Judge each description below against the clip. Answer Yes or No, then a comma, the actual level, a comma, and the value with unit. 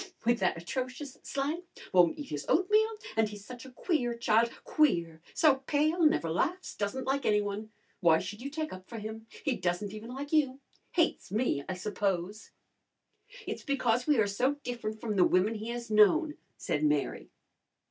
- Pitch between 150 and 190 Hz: No, high, 230 Hz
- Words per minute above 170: Yes, average, 180 wpm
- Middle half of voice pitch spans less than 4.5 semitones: No, wide, 5.6 semitones